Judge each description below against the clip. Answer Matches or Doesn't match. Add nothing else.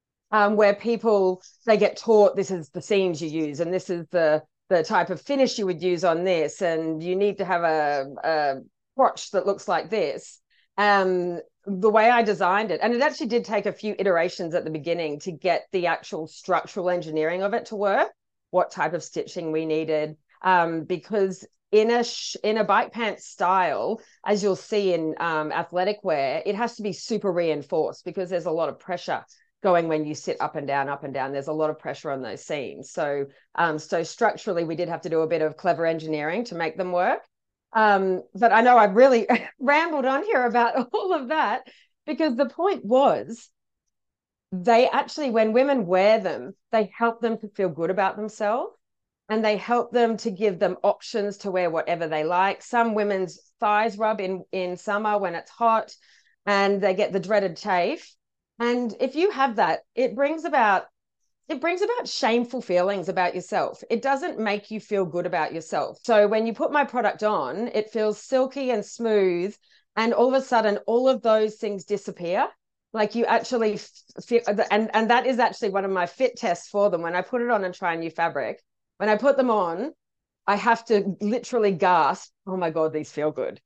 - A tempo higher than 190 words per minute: Matches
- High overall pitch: Matches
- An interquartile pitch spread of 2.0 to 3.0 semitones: Doesn't match